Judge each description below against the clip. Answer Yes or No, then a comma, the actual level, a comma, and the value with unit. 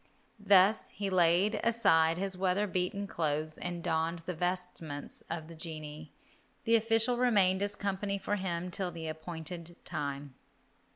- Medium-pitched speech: Yes, medium, 180 Hz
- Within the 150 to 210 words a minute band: No, average, 140 wpm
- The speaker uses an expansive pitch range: No, average, 3.6 semitones